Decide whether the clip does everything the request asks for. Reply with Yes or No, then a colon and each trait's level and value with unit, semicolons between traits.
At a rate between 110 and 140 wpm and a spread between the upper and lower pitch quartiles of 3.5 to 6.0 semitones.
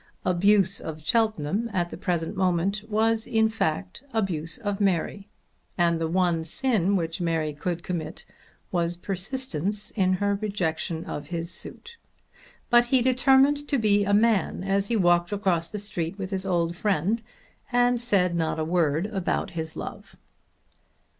No: average, 155 wpm; average, 4.1 semitones